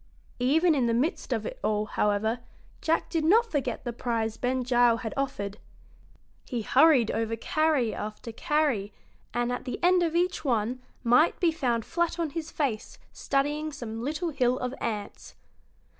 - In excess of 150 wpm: Yes, average, 165 wpm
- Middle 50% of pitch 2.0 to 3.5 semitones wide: No, wide, 5.5 semitones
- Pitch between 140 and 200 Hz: No, very high, 255 Hz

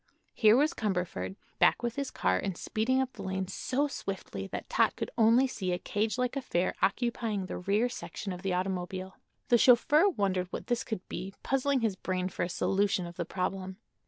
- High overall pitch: Yes, high, 200 Hz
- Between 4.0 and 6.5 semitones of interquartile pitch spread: Yes, average, 4.6 semitones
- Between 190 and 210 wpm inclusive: Yes, average, 195 wpm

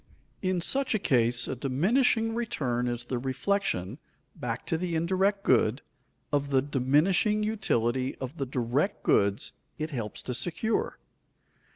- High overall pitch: No, medium, 140 Hz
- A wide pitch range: Yes, wide, 7.9 semitones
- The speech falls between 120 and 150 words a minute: Yes, average, 140 wpm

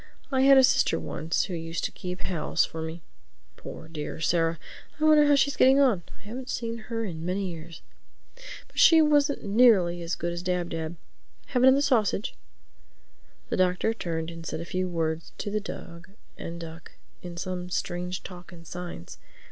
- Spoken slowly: No, average, 180 wpm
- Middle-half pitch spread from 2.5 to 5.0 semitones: No, wide, 5.5 semitones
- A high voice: No, medium, 180 Hz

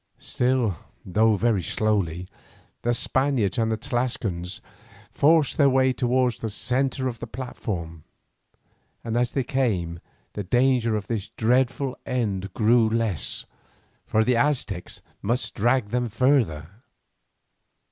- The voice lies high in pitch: No, low, 115 Hz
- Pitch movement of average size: Yes, average, 3.8 semitones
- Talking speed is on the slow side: Yes, slow, 120 wpm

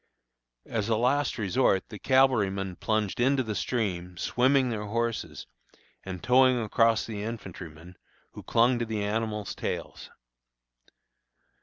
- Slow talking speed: Yes, slow, 125 wpm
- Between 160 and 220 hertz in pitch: No, low, 110 Hz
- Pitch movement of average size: Yes, average, 3.5 semitones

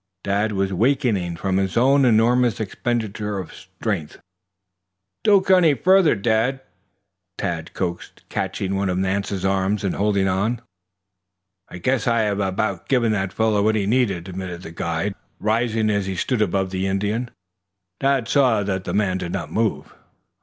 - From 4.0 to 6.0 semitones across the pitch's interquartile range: No, average, 3.5 semitones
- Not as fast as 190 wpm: Yes, average, 160 wpm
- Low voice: Yes, low, 105 Hz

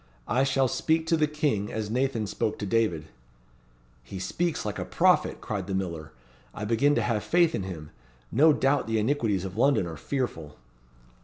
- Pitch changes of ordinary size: No, wide, 6.7 semitones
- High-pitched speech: No, low, 115 Hz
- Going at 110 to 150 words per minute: No, average, 180 wpm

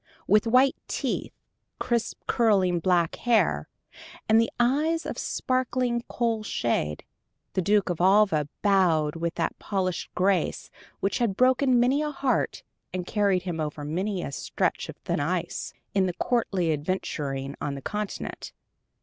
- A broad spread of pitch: Yes, wide, 5.9 semitones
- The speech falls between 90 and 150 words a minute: Yes, average, 140 wpm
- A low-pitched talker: No, high, 195 Hz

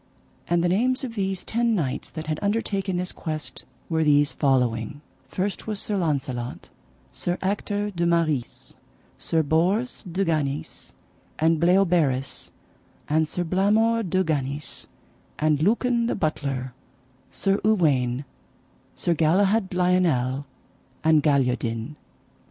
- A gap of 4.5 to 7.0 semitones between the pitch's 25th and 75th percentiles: Yes, average, 5.3 semitones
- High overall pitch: No, medium, 165 Hz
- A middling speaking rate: No, slow, 120 wpm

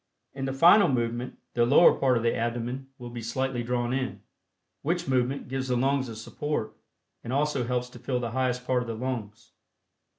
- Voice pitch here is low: Yes, low, 125 Hz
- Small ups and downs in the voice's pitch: Yes, narrow, 2.0 semitones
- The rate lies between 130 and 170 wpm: No, average, 195 wpm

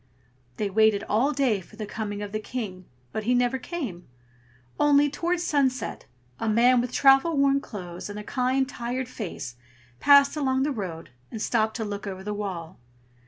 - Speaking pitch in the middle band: No, high, 230 Hz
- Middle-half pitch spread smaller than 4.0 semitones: No, average, 4.7 semitones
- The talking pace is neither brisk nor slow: Yes, average, 175 wpm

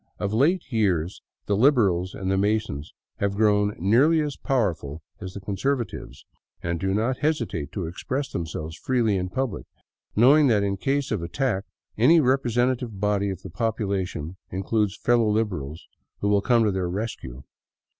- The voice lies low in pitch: Yes, low, 105 Hz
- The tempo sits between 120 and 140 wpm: No, average, 155 wpm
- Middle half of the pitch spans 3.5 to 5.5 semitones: Yes, average, 4.6 semitones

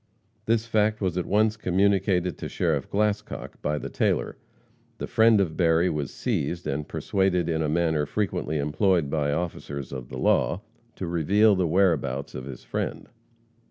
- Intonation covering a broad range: No, average, 5.0 semitones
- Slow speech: No, average, 160 wpm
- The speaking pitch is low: Yes, very low, 85 Hz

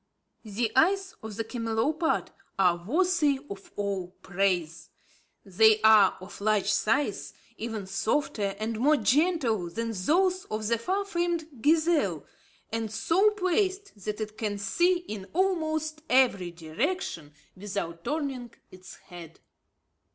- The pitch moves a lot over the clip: Yes, wide, 7.9 semitones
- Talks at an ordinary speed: No, slow, 125 wpm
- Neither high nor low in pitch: No, high, 225 Hz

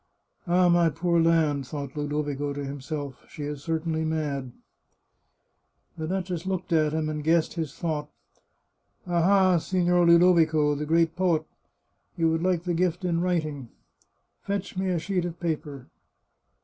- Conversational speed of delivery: Yes, average, 160 wpm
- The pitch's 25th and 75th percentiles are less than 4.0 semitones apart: Yes, average, 2.9 semitones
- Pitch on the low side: No, medium, 165 Hz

